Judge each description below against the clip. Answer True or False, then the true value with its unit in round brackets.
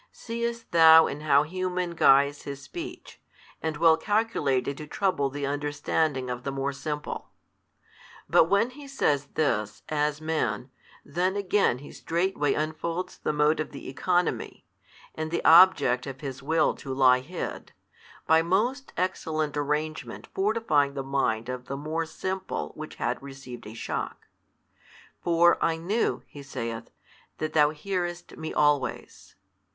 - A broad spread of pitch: False (4.1 semitones)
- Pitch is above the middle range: False (155 Hz)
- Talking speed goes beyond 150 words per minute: False (145 wpm)